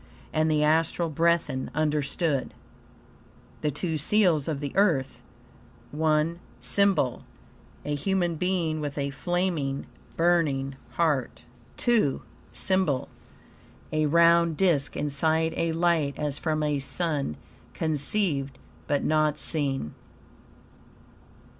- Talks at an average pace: No, slow, 105 wpm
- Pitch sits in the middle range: Yes, medium, 155 Hz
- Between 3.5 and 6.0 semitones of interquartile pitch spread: No, average, 2.9 semitones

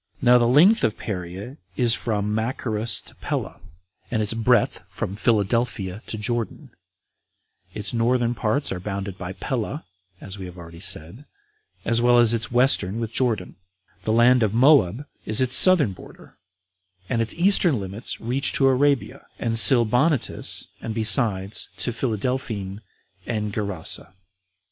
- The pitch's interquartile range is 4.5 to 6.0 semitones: No, average, 3.6 semitones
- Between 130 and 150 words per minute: Yes, average, 145 wpm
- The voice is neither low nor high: No, low, 115 Hz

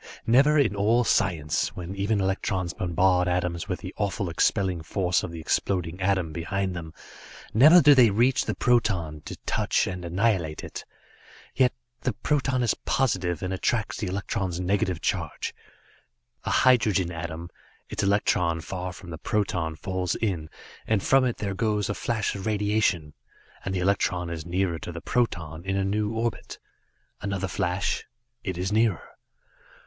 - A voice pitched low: Yes, very low, 95 Hz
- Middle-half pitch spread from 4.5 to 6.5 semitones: No, average, 3.5 semitones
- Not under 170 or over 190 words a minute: No, average, 160 wpm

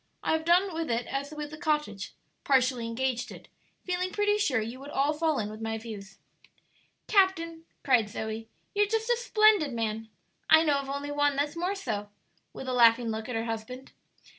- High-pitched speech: Yes, very high, 275 Hz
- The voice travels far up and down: Yes, wide, 6.4 semitones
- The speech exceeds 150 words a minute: Yes, average, 190 wpm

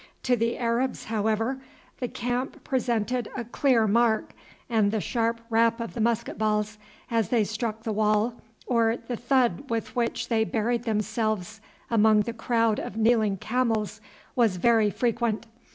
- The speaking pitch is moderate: No, high, 230 Hz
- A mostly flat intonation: Yes, narrow, 1.7 semitones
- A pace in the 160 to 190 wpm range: No, average, 150 wpm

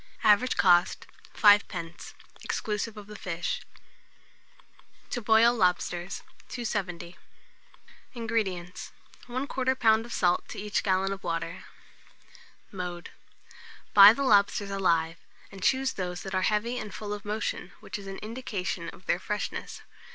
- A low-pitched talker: No, high, 200 Hz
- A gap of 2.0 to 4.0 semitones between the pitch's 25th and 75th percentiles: Yes, average, 3.5 semitones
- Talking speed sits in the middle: No, slow, 130 wpm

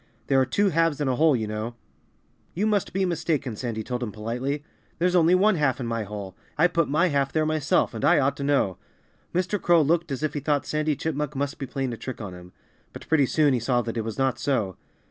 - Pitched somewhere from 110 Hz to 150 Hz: Yes, medium, 140 Hz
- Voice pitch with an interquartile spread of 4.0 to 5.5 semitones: Yes, average, 4.9 semitones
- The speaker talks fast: Yes, fast, 240 wpm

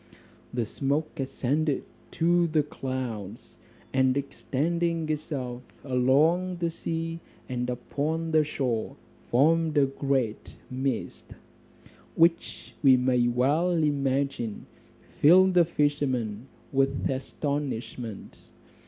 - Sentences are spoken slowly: Yes, slow, 95 wpm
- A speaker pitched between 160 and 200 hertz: No, medium, 140 Hz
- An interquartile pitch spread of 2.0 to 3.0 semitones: No, average, 4.0 semitones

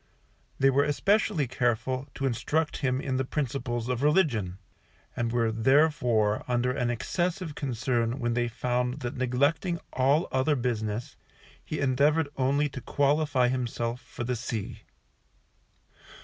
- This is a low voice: Yes, low, 130 Hz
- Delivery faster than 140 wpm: No, slow, 135 wpm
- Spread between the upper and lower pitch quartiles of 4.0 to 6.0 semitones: No, average, 3.1 semitones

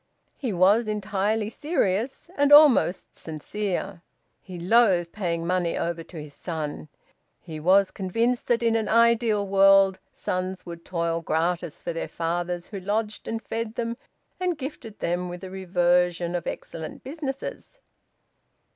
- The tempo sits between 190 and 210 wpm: No, average, 140 wpm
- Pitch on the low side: No, high, 190 Hz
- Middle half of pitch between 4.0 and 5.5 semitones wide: Yes, average, 4.5 semitones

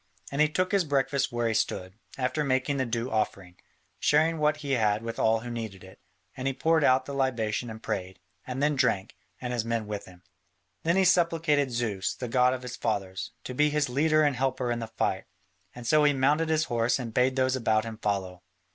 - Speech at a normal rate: No, fast, 220 wpm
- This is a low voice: Yes, low, 125 Hz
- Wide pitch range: No, average, 4.4 semitones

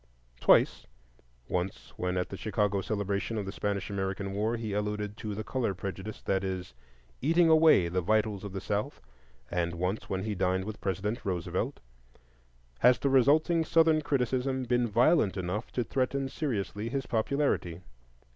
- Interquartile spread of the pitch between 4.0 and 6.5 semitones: Yes, average, 5.1 semitones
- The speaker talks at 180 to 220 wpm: No, average, 150 wpm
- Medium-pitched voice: No, low, 105 Hz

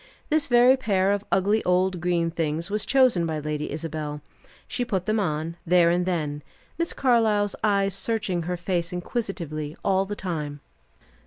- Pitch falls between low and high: Yes, medium, 180 Hz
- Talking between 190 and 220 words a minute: No, average, 160 wpm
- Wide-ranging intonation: No, average, 4.0 semitones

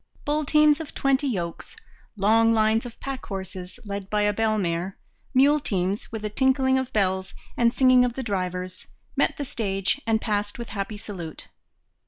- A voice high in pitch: Yes, high, 220 Hz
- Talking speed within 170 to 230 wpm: Yes, average, 175 wpm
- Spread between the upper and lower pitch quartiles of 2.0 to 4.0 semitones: No, average, 5.1 semitones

